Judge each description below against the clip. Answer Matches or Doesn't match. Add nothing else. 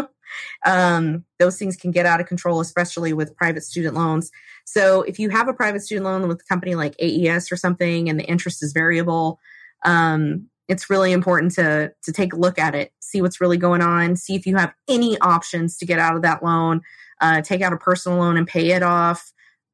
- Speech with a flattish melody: Matches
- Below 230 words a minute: Matches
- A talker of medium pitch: Matches